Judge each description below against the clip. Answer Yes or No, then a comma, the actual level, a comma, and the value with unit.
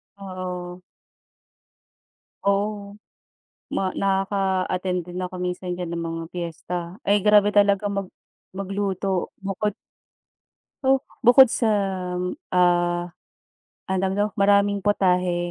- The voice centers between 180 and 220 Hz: Yes, high, 190 Hz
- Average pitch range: No, narrow, 2.0 semitones